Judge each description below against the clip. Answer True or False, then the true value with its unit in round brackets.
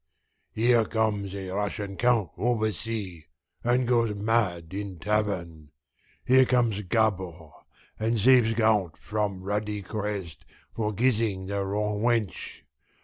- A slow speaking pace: True (115 wpm)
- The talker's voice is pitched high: False (105 Hz)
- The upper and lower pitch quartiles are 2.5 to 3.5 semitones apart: True (2.8 semitones)